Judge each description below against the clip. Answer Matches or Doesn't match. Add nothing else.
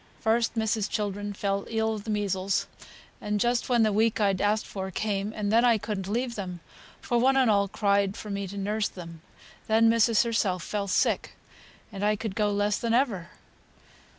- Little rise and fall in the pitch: Matches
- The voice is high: Matches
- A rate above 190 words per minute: Doesn't match